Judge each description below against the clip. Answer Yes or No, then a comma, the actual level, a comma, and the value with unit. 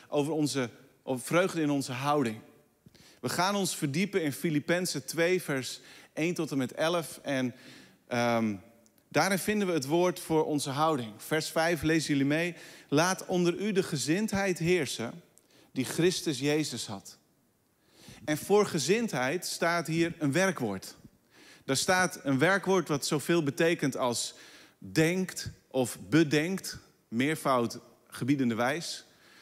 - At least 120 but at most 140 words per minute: Yes, slow, 135 wpm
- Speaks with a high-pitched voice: No, medium, 155 Hz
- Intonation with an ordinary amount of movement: Yes, average, 4.7 semitones